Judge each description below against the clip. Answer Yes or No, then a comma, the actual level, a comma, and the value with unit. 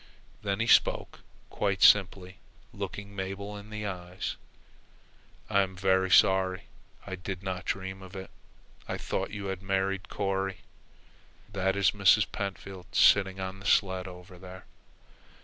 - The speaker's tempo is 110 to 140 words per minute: Yes, slow, 135 wpm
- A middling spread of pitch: No, narrow, 1.0 semitones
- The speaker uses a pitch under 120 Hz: Yes, very low, 95 Hz